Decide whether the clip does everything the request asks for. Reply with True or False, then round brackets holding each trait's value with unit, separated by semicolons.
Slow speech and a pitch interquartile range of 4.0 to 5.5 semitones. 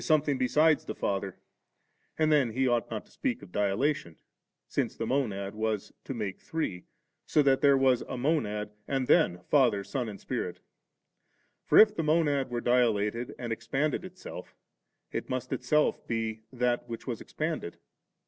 False (160 wpm; 5.0 semitones)